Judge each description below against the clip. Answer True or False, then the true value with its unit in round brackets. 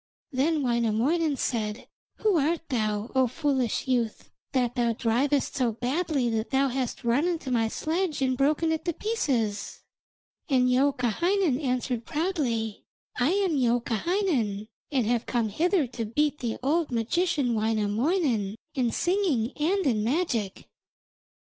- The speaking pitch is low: False (255 Hz)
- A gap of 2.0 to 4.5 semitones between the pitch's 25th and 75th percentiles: False (5.4 semitones)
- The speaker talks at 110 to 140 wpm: True (135 wpm)